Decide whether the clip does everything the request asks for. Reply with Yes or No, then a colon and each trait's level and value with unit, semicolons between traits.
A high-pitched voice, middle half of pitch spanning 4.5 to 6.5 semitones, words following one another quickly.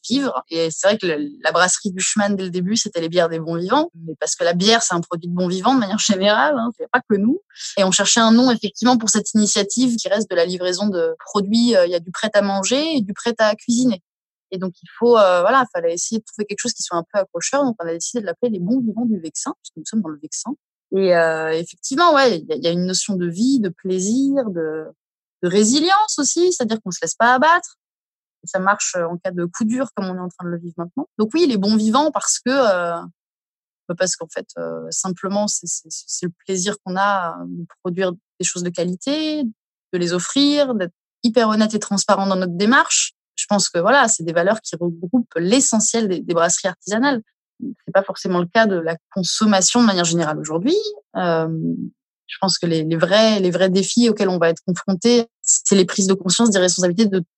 Yes: high, 195 Hz; average, 5.2 semitones; fast, 235 wpm